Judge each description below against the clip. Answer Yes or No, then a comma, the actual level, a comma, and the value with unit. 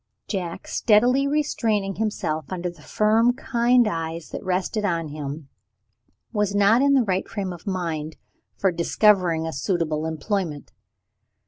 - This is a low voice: No, medium, 185 Hz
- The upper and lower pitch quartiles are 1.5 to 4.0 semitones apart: No, average, 4.7 semitones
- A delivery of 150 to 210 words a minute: No, slow, 135 wpm